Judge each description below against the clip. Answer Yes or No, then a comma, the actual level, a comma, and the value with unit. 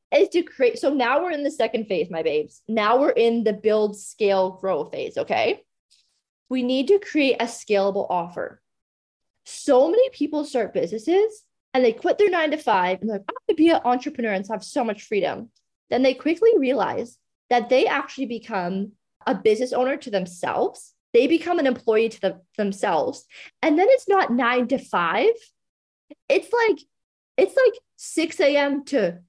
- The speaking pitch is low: No, very high, 255 Hz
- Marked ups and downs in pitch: Yes, wide, 7.3 semitones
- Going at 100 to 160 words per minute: No, average, 180 wpm